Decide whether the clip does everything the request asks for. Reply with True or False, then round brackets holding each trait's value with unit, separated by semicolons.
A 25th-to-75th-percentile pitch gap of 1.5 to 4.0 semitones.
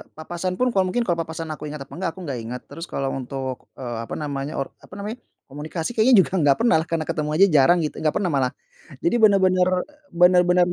False (4.4 semitones)